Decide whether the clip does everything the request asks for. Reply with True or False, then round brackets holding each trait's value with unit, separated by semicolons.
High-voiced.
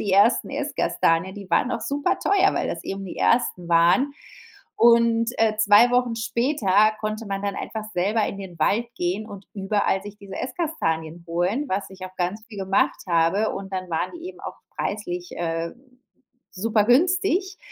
True (205 Hz)